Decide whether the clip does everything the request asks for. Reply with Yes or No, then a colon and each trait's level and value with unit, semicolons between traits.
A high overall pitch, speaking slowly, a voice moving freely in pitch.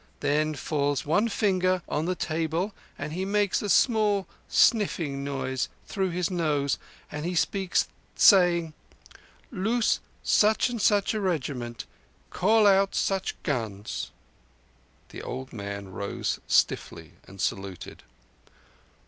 No: medium, 170 Hz; slow, 120 wpm; wide, 5.9 semitones